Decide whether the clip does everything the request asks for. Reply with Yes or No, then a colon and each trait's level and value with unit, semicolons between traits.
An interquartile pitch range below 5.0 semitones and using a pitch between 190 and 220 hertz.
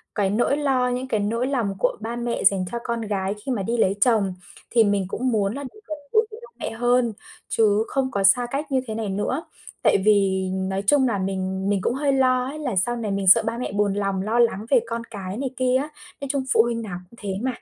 No: average, 4.3 semitones; high, 230 Hz